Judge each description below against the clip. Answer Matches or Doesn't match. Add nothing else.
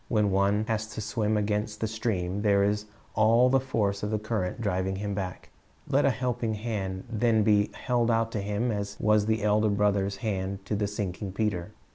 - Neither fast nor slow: Matches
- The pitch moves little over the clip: Matches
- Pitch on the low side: Matches